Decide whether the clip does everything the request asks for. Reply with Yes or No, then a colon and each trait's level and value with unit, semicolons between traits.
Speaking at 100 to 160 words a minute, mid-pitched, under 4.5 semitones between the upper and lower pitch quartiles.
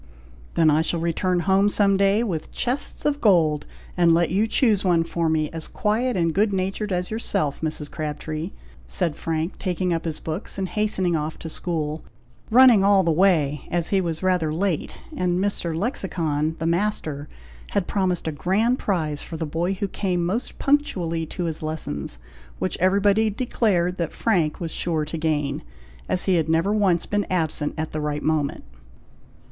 No: average, 175 wpm; medium, 175 Hz; average, 3.7 semitones